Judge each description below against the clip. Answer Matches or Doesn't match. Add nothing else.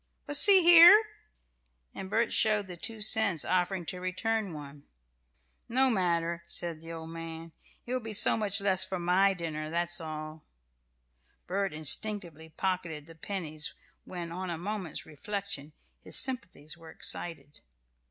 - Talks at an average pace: Matches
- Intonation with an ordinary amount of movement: Matches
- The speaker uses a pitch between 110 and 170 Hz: Doesn't match